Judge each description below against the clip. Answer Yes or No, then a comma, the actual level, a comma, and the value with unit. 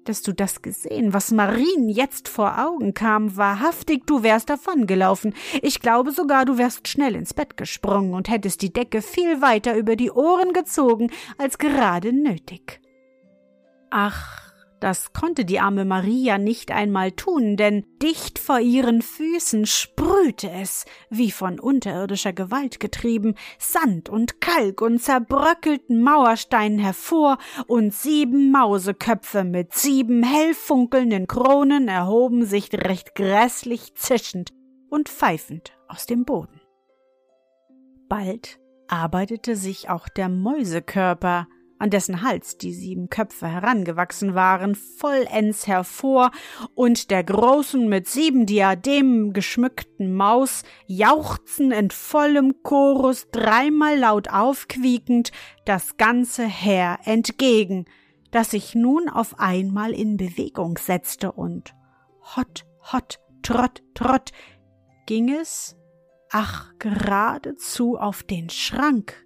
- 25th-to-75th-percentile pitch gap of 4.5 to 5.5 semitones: Yes, average, 5.2 semitones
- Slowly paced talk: Yes, slow, 120 wpm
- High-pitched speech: Yes, high, 225 Hz